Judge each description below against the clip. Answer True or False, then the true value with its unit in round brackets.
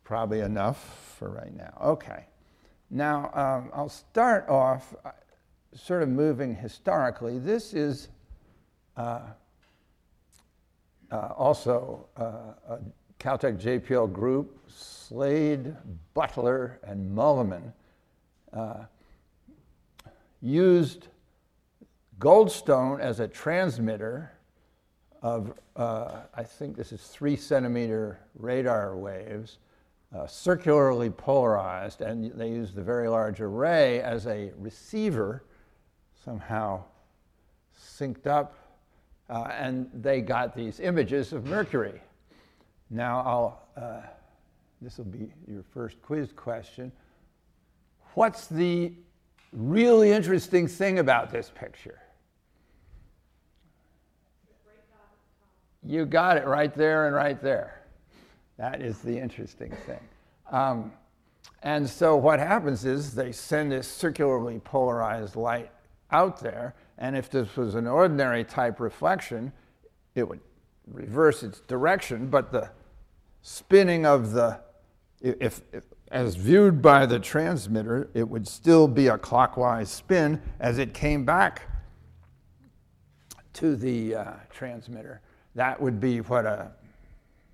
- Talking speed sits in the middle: False (110 wpm)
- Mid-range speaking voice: False (125 Hz)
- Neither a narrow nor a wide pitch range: True (4.7 semitones)